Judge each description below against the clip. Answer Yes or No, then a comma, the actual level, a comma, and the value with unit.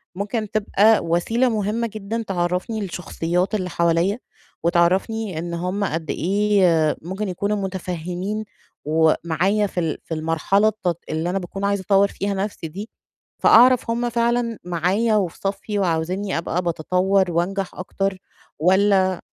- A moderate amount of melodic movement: Yes, average, 3.3 semitones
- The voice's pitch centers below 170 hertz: No, high, 190 Hz